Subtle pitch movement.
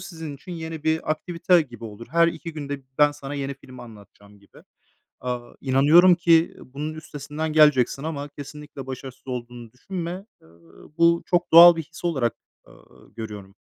No: average, 4.5 semitones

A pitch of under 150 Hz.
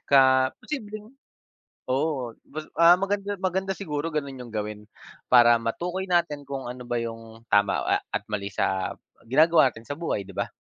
Yes: medium, 140 Hz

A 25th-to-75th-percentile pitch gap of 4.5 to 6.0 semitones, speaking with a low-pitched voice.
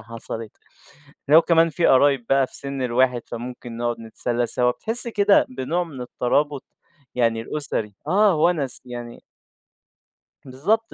Yes: average, 5.2 semitones; low, 130 Hz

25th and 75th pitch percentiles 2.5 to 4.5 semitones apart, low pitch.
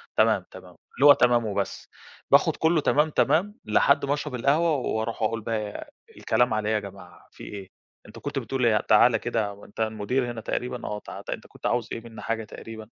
Yes: average, 2.9 semitones; low, 115 Hz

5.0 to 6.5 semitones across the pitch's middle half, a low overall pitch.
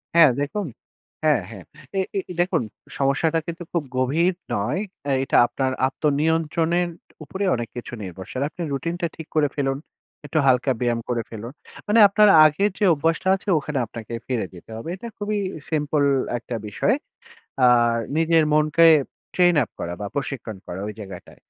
No: wide, 5.6 semitones; medium, 145 Hz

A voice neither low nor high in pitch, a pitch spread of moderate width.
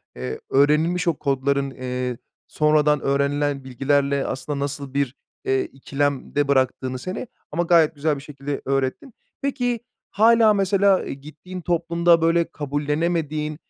Yes: medium, 145 Hz; average, 3.5 semitones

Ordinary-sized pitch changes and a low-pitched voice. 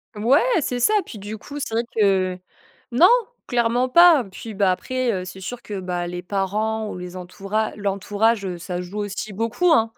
No: average, 3.9 semitones; high, 210 Hz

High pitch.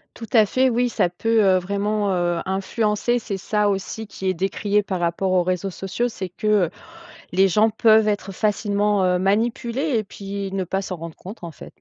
Yes: high, 200 Hz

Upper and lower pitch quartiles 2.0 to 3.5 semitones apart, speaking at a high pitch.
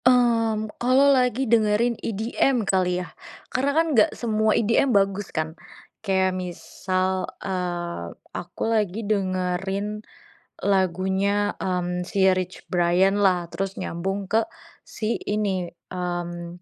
Yes: average, 3.2 semitones; high, 195 Hz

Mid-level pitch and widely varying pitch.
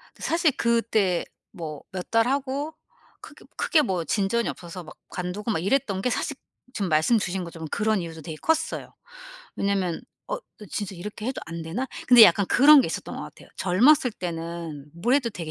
No: high, 200 Hz; wide, 6.4 semitones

